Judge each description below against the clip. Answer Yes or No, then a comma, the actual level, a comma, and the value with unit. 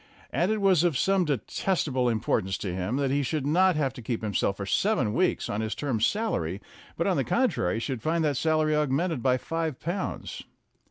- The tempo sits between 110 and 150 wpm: No, average, 200 wpm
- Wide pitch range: Yes, wide, 6.5 semitones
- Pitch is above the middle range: No, medium, 140 Hz